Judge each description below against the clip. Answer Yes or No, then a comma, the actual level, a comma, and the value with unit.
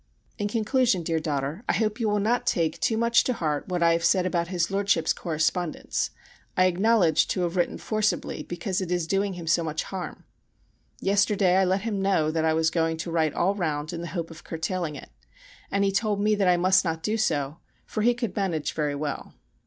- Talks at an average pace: No, fast, 215 wpm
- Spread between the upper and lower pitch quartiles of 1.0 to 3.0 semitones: No, average, 3.8 semitones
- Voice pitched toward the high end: No, medium, 180 Hz